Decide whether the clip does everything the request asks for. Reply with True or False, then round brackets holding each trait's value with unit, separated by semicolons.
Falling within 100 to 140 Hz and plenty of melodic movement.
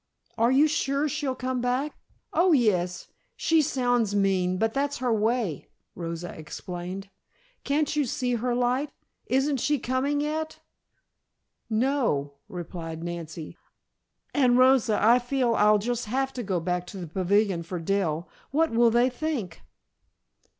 False (240 Hz; 6.6 semitones)